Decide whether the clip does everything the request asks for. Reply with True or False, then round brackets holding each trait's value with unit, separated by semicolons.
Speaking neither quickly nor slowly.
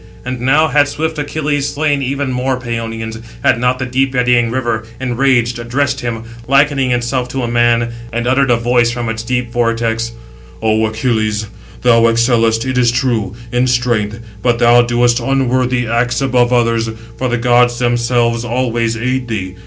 True (165 wpm)